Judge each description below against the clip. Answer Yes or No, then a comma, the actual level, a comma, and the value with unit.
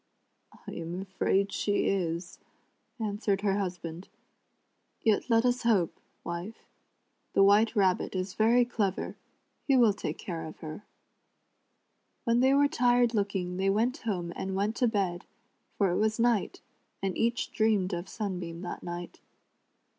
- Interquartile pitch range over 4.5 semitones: No, average, 4.0 semitones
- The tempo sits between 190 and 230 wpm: No, average, 150 wpm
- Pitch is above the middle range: Yes, high, 200 Hz